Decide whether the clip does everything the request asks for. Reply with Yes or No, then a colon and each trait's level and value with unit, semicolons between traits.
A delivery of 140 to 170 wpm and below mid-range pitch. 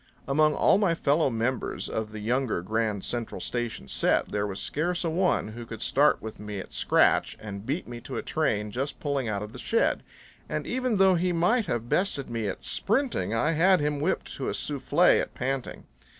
No: fast, 205 wpm; low, 130 Hz